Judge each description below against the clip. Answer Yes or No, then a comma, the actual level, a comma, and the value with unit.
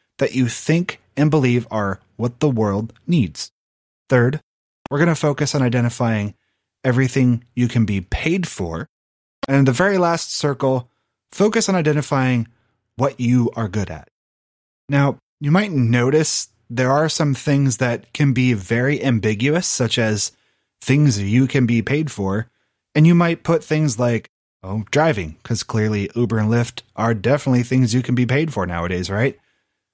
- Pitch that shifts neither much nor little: Yes, average, 4.7 semitones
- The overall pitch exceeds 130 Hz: No, low, 125 Hz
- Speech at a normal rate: Yes, average, 160 wpm